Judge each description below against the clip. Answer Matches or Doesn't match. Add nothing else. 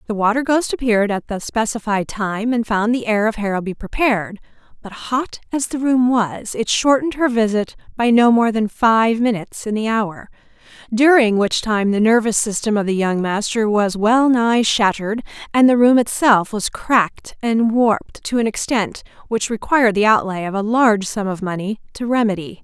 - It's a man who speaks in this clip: Doesn't match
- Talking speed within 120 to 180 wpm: Doesn't match